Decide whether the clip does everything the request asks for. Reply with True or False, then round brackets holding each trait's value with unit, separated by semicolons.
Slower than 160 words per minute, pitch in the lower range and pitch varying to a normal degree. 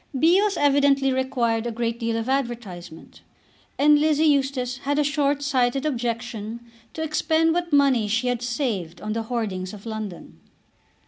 False (150 wpm; 250 Hz; 4.1 semitones)